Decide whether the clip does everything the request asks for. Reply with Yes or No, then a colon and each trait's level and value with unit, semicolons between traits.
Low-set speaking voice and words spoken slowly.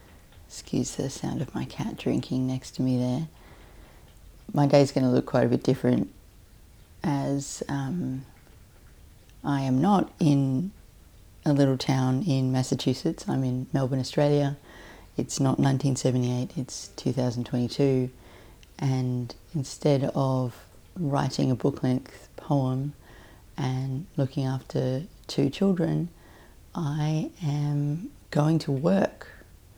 Yes: low, 130 Hz; slow, 115 wpm